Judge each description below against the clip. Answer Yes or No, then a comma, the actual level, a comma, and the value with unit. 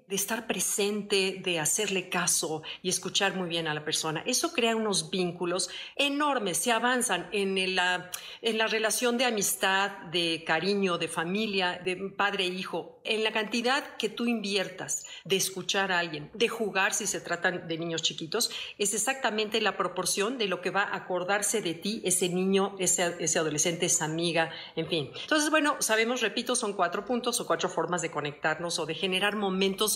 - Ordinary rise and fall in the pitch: Yes, average, 3.8 semitones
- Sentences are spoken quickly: No, average, 180 wpm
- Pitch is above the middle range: Yes, high, 195 Hz